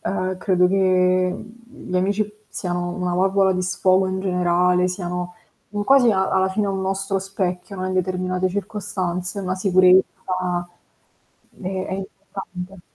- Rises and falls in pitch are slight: Yes, narrow, 1.1 semitones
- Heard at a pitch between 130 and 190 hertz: Yes, medium, 185 Hz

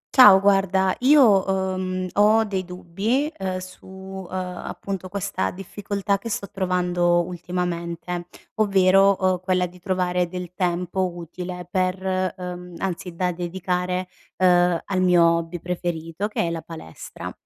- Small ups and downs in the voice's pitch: Yes, narrow, 1.5 semitones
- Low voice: No, medium, 185 Hz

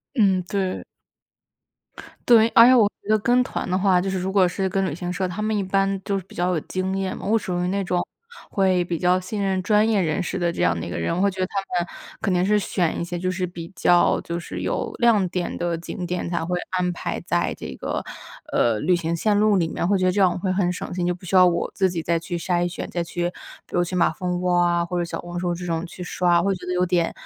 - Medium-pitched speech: Yes, medium, 180 Hz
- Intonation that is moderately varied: No, narrow, 1.8 semitones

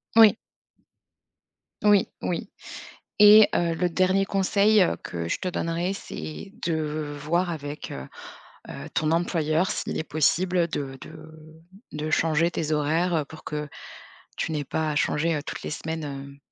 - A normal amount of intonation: Yes, average, 3.1 semitones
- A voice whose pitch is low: No, medium, 160 Hz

